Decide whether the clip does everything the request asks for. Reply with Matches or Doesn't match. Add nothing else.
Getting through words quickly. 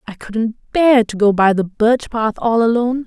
Matches